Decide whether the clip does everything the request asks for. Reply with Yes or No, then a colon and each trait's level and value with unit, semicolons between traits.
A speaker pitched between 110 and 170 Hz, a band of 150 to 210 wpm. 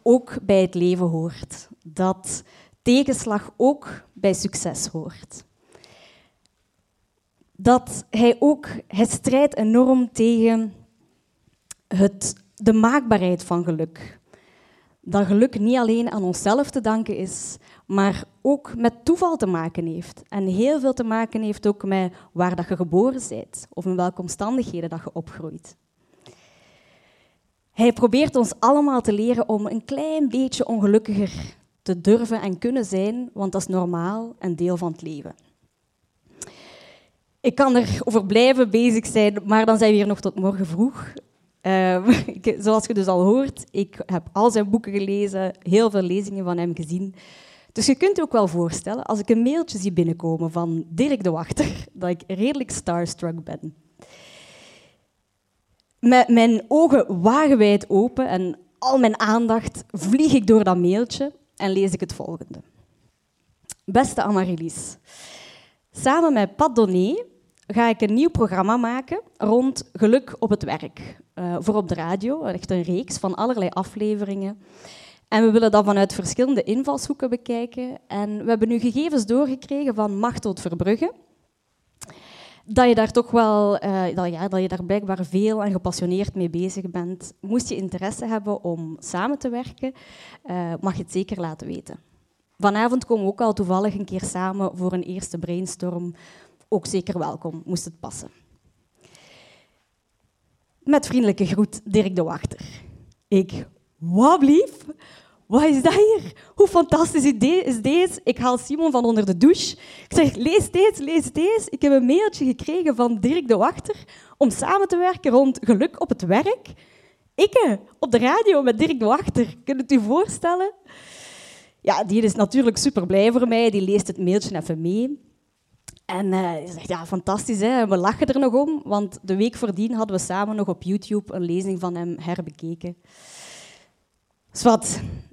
No: high, 210 Hz; average, 160 wpm